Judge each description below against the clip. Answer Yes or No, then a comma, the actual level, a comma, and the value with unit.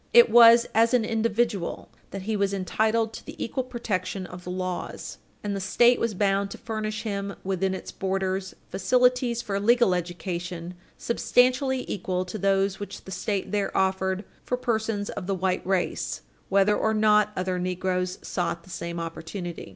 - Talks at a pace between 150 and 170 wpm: Yes, average, 165 wpm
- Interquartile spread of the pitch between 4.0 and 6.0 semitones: No, average, 3.3 semitones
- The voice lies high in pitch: Yes, high, 195 Hz